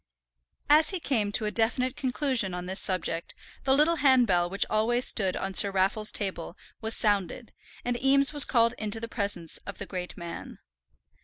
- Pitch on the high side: Yes, high, 215 Hz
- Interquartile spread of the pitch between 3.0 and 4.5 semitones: No, average, 4.9 semitones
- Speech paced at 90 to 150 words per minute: No, average, 175 wpm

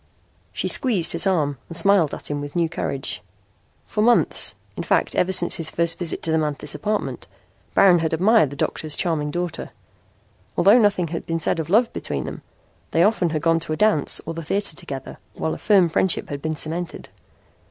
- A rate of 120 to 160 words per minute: No, average, 195 wpm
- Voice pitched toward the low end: No, medium, 165 Hz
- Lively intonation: No, average, 3.4 semitones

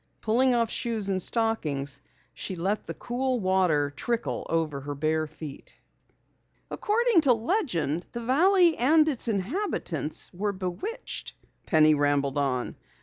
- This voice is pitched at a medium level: No, high, 200 Hz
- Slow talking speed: Yes, slow, 130 wpm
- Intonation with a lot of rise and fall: Yes, wide, 8.7 semitones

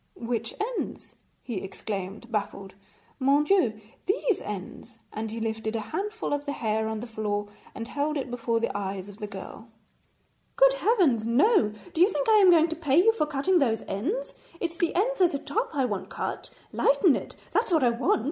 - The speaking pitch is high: Yes, very high, 250 Hz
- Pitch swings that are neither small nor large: No, wide, 8.1 semitones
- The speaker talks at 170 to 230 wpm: Yes, average, 195 wpm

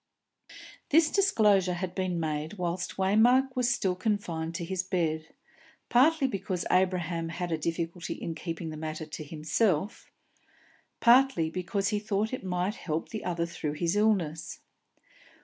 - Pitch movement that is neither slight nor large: Yes, average, 4.2 semitones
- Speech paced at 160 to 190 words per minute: No, average, 145 wpm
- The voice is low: No, medium, 180 Hz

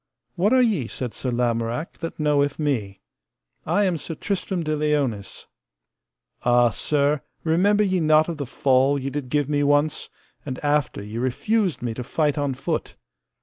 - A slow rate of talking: No, average, 165 wpm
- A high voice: No, medium, 145 Hz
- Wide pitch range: No, average, 4.1 semitones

